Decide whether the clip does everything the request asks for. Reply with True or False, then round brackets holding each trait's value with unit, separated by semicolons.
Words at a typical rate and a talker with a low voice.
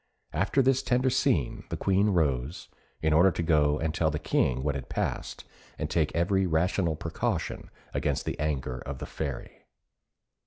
True (165 wpm; 80 Hz)